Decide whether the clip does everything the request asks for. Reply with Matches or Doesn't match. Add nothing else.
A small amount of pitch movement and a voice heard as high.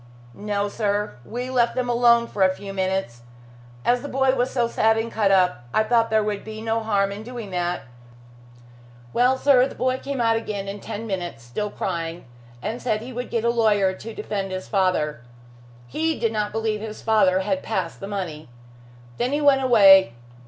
Doesn't match